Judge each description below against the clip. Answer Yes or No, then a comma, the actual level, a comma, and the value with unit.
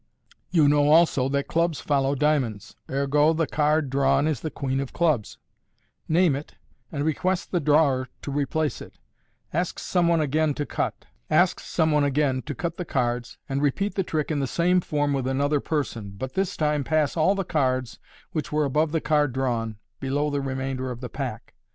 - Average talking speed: Yes, average, 180 wpm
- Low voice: No, medium, 145 Hz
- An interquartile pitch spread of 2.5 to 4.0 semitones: Yes, average, 2.8 semitones